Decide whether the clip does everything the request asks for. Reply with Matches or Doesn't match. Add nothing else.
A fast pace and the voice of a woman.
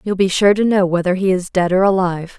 Matches